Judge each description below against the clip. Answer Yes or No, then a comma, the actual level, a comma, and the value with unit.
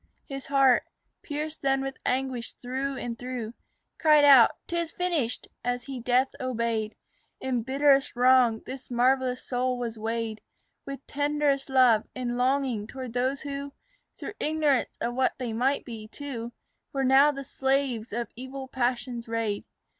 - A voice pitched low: No, very high, 255 Hz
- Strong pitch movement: No, narrow, 2.5 semitones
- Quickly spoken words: No, average, 145 wpm